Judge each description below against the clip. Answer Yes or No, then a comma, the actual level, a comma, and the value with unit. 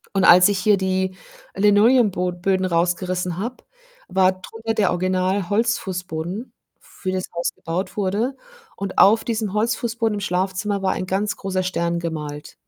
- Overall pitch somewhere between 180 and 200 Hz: Yes, high, 190 Hz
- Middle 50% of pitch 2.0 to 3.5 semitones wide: Yes, narrow, 2.5 semitones